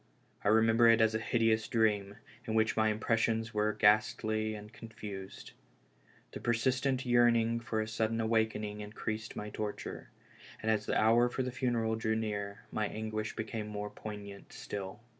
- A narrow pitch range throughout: Yes, narrow, 1.3 semitones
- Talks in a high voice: No, low, 110 Hz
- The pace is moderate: Yes, average, 160 wpm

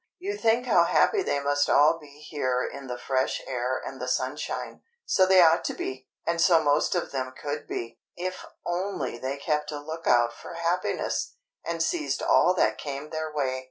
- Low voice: No, medium, 150 Hz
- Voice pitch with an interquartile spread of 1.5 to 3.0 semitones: No, average, 4.3 semitones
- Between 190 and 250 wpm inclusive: Yes, average, 195 wpm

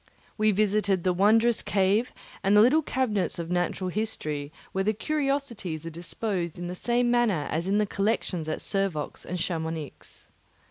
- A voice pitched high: Yes, high, 195 Hz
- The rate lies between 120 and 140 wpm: No, average, 160 wpm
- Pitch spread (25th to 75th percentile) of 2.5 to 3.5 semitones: No, average, 4.2 semitones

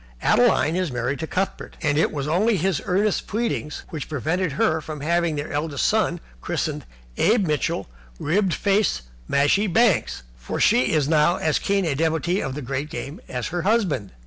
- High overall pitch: No, medium, 160 Hz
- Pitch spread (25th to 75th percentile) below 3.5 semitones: No, average, 4.4 semitones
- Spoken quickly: No, average, 175 wpm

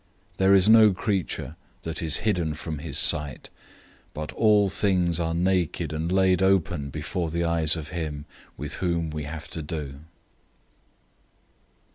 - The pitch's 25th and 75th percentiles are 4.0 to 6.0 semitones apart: No, average, 3.4 semitones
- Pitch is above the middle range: No, very low, 85 Hz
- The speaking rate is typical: Yes, average, 150 wpm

